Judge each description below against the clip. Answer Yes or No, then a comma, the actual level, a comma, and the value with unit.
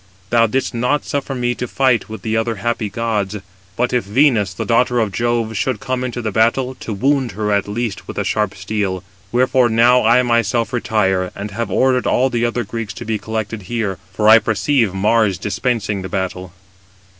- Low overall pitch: Yes, low, 115 Hz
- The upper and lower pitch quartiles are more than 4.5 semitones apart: No, average, 2.9 semitones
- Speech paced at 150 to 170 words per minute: No, average, 195 wpm